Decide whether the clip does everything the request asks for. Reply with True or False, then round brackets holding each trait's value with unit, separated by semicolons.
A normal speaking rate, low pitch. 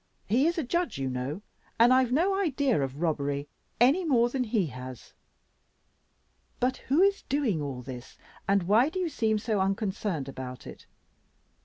False (165 wpm; 220 Hz)